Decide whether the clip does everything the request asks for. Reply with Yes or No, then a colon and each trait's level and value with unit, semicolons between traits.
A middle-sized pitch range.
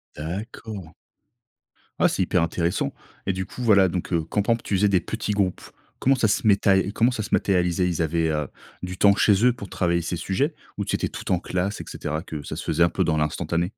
Yes: average, 3.4 semitones